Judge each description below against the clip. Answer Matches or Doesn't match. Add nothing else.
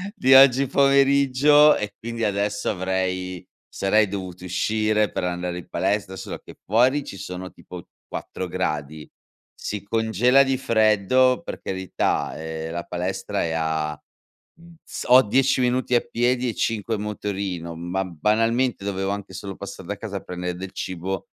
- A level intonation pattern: Doesn't match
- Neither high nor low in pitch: Doesn't match